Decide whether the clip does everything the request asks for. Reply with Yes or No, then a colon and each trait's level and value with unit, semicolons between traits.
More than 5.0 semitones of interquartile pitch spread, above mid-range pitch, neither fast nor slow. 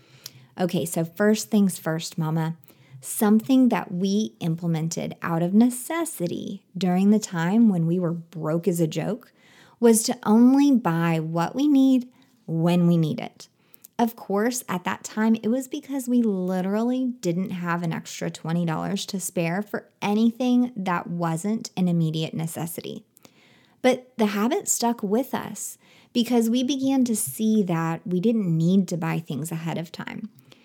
Yes: wide, 5.6 semitones; high, 195 Hz; average, 155 wpm